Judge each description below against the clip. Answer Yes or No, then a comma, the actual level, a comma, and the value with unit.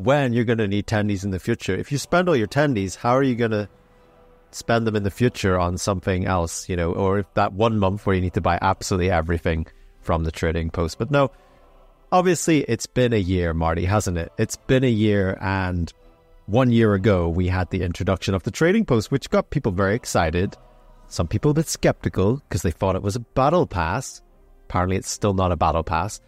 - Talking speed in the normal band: No, fast, 220 wpm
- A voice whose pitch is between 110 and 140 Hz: No, low, 100 Hz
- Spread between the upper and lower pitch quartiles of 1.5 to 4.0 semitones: No, average, 5.0 semitones